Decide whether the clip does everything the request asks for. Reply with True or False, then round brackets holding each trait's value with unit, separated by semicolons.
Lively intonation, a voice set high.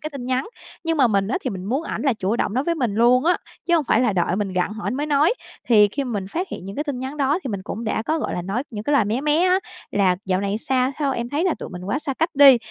True (6.0 semitones; 250 Hz)